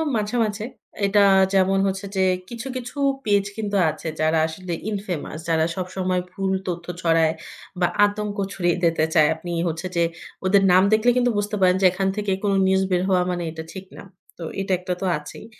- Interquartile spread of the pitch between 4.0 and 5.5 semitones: No, average, 2.9 semitones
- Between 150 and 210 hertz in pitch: Yes, high, 190 Hz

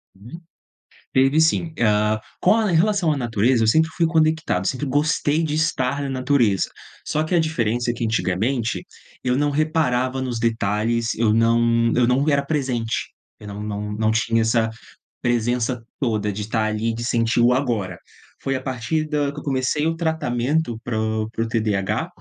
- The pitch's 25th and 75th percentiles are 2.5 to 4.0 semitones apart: No, average, 4.6 semitones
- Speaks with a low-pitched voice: Yes, low, 120 Hz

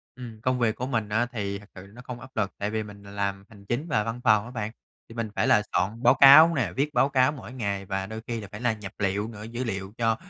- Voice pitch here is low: Yes, low, 110 Hz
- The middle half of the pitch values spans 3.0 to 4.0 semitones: Yes, average, 3.3 semitones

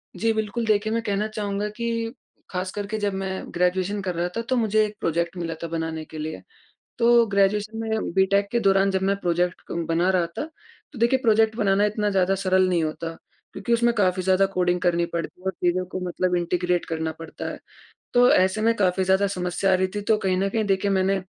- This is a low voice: No, high, 195 Hz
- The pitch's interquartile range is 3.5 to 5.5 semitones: No, average, 3.0 semitones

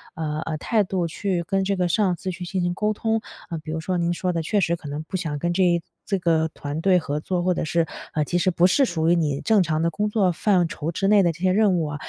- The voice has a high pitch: No, medium, 175 Hz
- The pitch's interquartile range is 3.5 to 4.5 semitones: No, average, 2.9 semitones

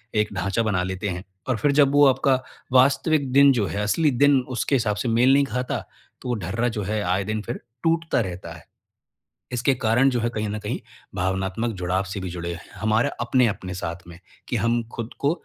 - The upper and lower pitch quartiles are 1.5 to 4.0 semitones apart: No, average, 5.1 semitones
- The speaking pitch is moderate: No, low, 110 Hz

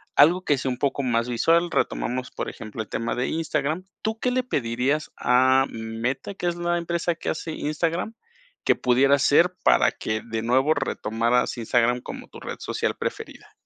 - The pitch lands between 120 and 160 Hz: Yes, low, 135 Hz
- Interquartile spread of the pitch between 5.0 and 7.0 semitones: Yes, wide, 5.6 semitones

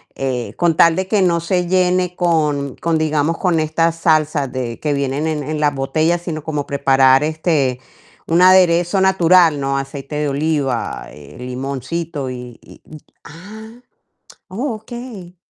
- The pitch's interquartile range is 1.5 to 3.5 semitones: No, average, 4.2 semitones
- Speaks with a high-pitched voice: No, medium, 155 Hz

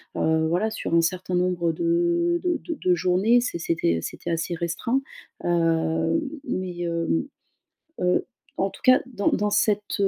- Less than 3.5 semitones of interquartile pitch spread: No, wide, 5.6 semitones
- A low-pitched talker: No, medium, 180 Hz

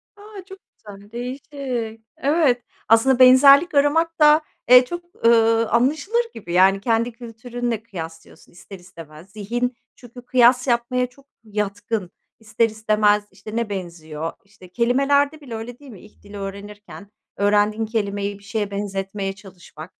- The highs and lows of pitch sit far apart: No, average, 3.8 semitones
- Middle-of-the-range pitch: No, high, 225 Hz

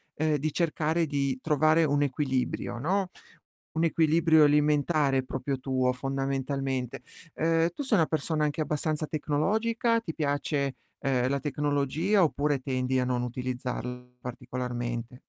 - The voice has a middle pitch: Yes, medium, 145 Hz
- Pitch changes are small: No, average, 3.4 semitones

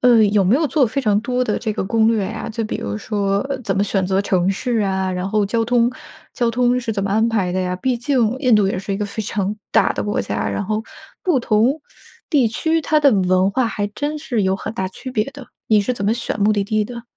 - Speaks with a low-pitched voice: No, high, 215 Hz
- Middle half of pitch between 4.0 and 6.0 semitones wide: No, average, 3.6 semitones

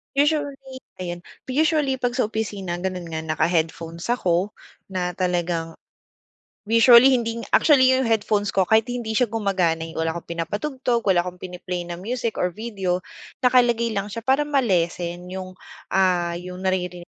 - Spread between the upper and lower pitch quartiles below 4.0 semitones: No, average, 5.3 semitones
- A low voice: No, high, 195 Hz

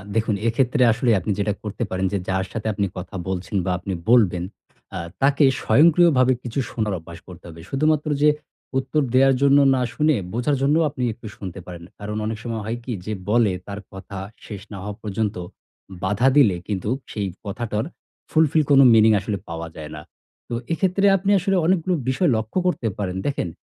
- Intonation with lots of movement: Yes, wide, 5.9 semitones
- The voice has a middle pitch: No, low, 110 Hz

